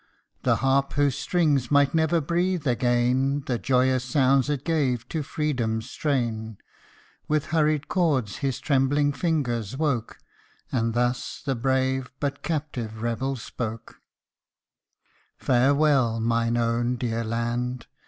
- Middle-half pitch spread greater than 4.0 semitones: No, average, 3.3 semitones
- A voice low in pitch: Yes, low, 130 Hz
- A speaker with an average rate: No, slow, 120 wpm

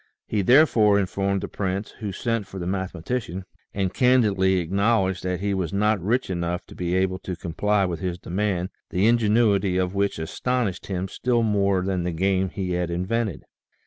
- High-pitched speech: No, very low, 95 Hz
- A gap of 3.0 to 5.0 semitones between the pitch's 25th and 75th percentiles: No, narrow, 2.5 semitones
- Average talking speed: Yes, average, 180 wpm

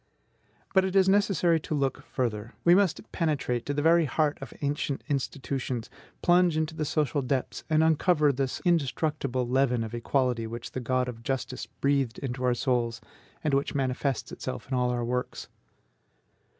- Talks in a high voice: No, low, 135 Hz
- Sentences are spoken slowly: No, average, 165 wpm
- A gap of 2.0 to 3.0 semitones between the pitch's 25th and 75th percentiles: No, average, 3.9 semitones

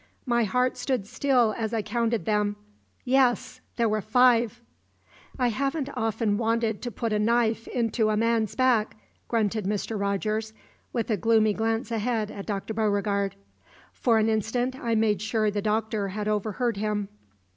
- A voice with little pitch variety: Yes, narrow, 2.0 semitones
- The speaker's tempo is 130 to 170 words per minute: Yes, average, 155 wpm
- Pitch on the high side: Yes, high, 220 Hz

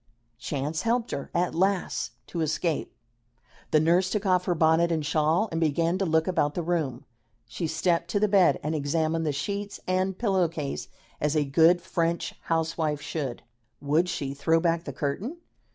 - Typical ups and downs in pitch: Yes, average, 3.0 semitones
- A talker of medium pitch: Yes, medium, 165 Hz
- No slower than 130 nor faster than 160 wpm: No, average, 175 wpm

